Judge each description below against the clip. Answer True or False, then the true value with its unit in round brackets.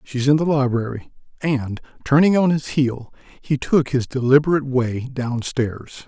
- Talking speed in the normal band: True (160 wpm)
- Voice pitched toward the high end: False (135 Hz)